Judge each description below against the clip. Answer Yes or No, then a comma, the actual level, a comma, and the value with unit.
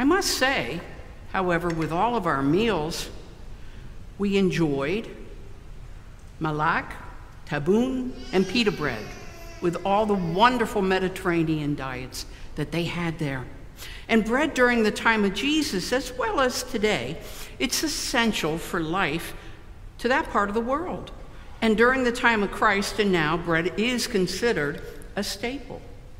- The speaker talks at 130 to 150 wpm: Yes, slow, 135 wpm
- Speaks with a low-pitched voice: No, high, 200 Hz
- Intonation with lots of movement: Yes, wide, 6.5 semitones